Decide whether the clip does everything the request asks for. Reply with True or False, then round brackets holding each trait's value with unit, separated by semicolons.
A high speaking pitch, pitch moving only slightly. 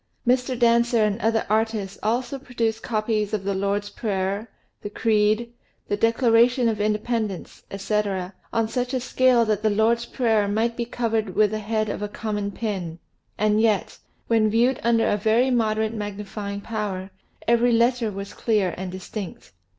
True (220 Hz; 2.2 semitones)